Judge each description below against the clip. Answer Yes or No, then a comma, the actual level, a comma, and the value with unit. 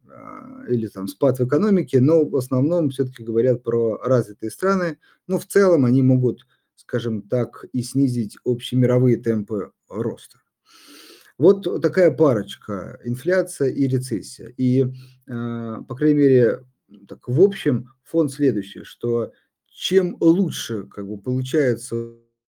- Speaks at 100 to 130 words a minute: Yes, average, 125 wpm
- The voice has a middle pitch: No, low, 130 Hz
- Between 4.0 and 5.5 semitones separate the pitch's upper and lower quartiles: Yes, average, 5.0 semitones